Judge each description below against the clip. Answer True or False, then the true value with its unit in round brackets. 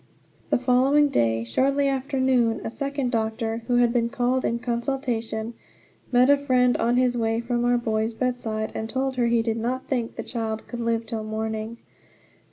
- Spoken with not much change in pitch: True (2.3 semitones)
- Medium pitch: False (240 Hz)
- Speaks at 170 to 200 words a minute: True (180 wpm)